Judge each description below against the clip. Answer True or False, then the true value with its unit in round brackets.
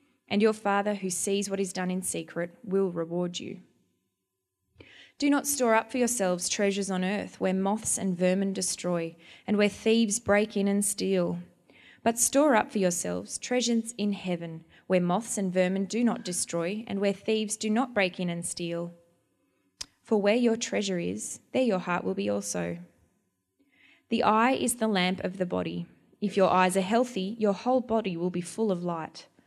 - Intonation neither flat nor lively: True (4.0 semitones)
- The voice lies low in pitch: False (195 Hz)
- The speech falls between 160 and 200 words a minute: True (185 wpm)